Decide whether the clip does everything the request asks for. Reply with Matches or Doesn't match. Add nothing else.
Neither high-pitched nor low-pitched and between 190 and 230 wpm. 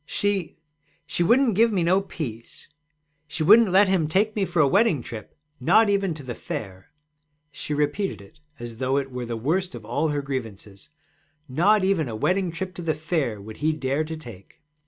Matches